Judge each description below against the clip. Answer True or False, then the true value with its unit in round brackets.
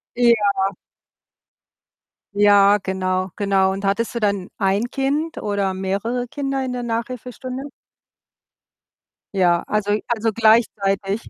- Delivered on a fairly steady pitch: False (3.5 semitones)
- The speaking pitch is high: True (205 Hz)